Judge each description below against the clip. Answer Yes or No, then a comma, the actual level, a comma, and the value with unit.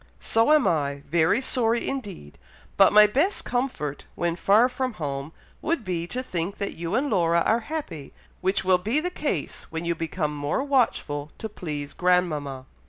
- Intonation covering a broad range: Yes, wide, 7.7 semitones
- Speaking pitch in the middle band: Yes, medium, 180 Hz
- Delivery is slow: No, average, 170 wpm